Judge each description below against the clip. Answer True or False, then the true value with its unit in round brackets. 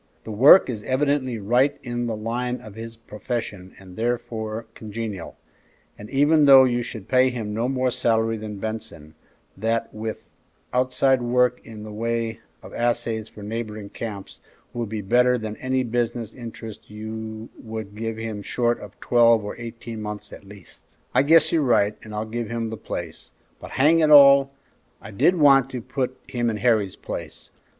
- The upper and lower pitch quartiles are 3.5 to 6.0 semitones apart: False (2.5 semitones)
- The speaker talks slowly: False (175 wpm)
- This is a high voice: False (115 Hz)